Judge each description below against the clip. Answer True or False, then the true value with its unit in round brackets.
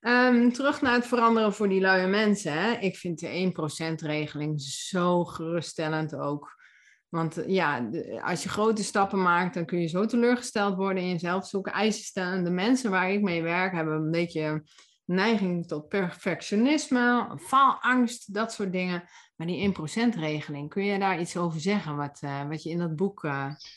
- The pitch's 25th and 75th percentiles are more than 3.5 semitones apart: True (4.2 semitones)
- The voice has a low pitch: False (180 Hz)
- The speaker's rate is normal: True (175 wpm)